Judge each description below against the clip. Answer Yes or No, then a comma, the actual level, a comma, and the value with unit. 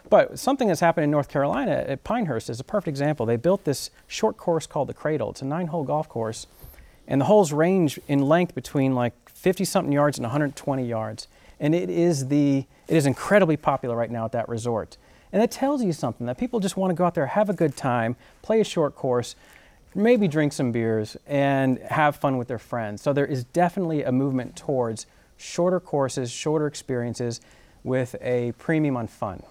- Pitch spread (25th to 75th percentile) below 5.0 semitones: No, wide, 5.6 semitones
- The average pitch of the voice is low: No, medium, 145 Hz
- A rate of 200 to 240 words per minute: Yes, fast, 205 wpm